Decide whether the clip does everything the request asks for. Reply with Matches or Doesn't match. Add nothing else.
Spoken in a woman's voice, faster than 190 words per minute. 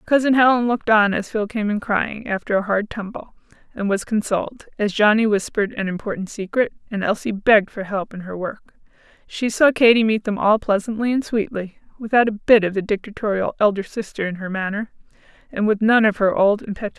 Matches